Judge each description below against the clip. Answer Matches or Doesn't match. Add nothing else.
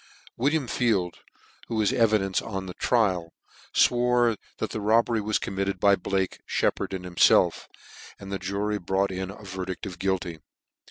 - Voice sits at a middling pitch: Doesn't match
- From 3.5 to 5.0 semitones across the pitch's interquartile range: Doesn't match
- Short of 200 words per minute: Matches